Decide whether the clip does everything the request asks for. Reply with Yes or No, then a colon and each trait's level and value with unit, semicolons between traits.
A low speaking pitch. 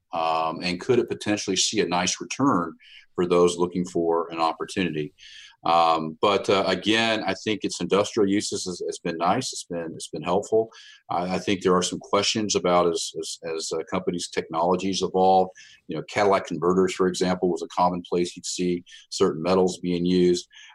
Yes: very low, 90 Hz